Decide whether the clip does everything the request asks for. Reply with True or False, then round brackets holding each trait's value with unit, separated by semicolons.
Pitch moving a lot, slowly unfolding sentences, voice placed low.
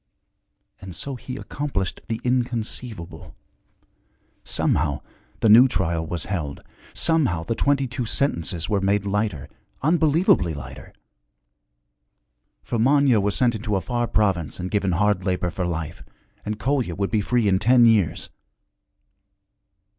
True (5.7 semitones; 130 wpm; 105 Hz)